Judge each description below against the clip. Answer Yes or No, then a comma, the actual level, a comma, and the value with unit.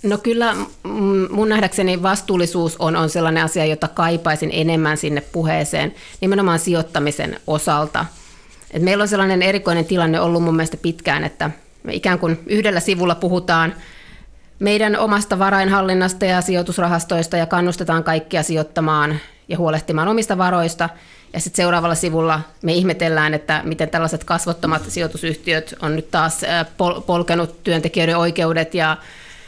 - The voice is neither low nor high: Yes, medium, 170 Hz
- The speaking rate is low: No, average, 130 wpm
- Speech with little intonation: Yes, narrow, 2.2 semitones